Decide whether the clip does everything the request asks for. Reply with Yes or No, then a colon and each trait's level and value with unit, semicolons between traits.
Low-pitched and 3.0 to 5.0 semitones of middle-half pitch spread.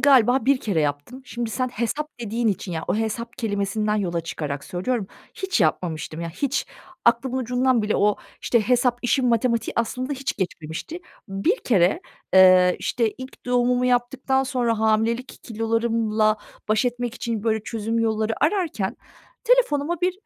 No: high, 230 Hz; average, 3.6 semitones